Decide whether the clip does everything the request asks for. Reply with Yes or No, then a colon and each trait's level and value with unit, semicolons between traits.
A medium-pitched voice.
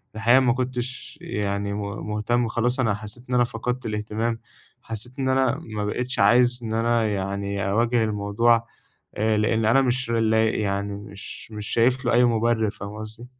No: low, 115 Hz